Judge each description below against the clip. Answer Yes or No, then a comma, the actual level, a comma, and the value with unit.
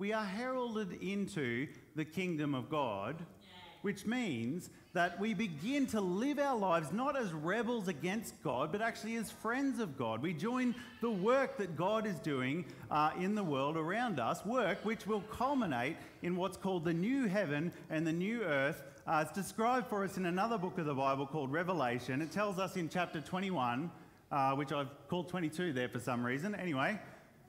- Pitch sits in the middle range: Yes, medium, 180 Hz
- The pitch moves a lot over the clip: Yes, wide, 5.9 semitones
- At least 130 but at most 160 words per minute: No, average, 185 wpm